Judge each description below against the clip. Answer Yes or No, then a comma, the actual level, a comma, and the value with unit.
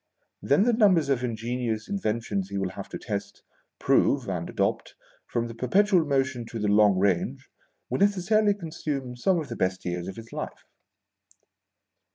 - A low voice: Yes, low, 125 Hz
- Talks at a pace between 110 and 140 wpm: No, average, 165 wpm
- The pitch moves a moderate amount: No, wide, 8.7 semitones